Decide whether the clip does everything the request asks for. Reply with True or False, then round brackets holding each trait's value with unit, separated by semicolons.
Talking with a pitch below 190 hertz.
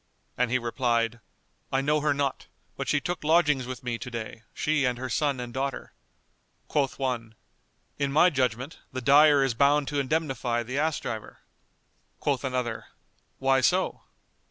True (135 Hz)